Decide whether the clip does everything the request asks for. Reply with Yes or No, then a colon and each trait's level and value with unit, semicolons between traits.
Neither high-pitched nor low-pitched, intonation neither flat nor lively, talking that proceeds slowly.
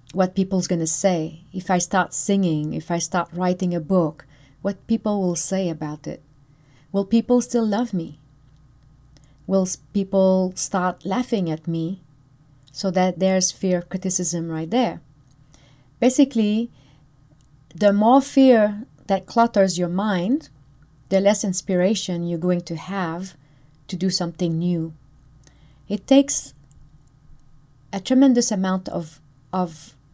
Yes: medium, 180 Hz; average, 4.8 semitones; slow, 130 wpm